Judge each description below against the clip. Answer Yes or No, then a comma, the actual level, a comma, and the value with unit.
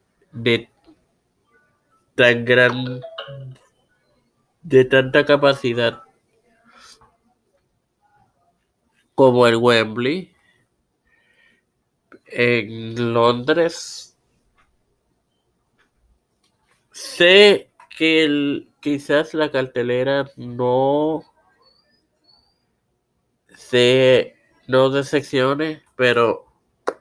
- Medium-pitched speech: No, low, 130 Hz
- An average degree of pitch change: Yes, average, 3.3 semitones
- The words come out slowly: Yes, slow, 50 wpm